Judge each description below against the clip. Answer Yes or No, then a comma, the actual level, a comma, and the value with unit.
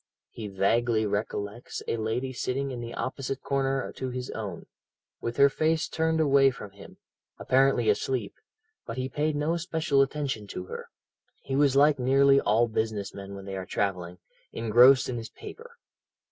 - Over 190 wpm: No, average, 165 wpm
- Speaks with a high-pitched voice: No, low, 130 Hz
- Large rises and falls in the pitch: No, average, 4.1 semitones